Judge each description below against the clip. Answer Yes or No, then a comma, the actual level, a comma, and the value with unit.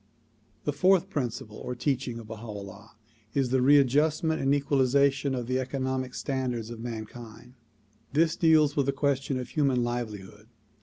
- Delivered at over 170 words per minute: No, average, 155 wpm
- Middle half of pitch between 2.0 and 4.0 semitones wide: Yes, average, 3.1 semitones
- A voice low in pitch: Yes, low, 130 Hz